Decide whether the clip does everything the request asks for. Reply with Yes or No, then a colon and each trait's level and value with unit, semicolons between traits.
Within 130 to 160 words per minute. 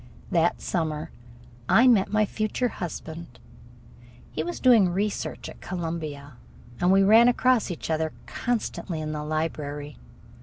Yes: average, 140 wpm